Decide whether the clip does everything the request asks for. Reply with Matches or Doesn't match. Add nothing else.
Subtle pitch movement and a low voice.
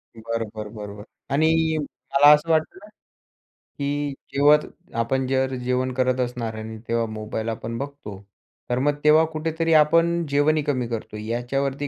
Doesn't match